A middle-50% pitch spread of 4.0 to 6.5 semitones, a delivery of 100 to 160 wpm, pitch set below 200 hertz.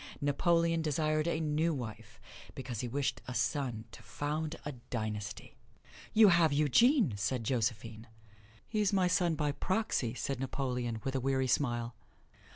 Yes: average, 5.1 semitones; average, 145 wpm; medium, 140 Hz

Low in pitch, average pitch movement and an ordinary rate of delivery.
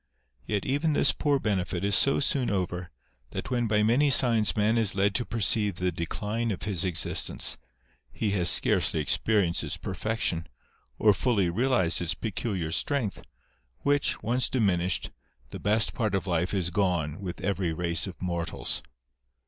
Yes: low, 100 Hz; average, 4.5 semitones; average, 155 wpm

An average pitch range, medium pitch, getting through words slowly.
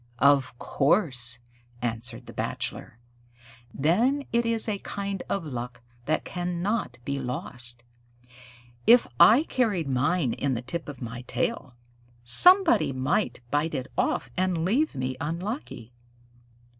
No: wide, 8.2 semitones; medium, 150 Hz; slow, 125 wpm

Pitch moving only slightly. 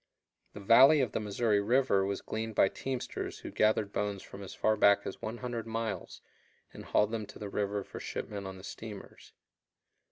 Yes: narrow, 2.2 semitones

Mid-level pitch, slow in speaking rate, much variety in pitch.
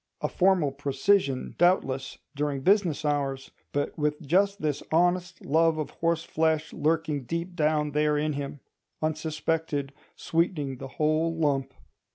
No: medium, 155 Hz; slow, 125 wpm; narrow, 2.6 semitones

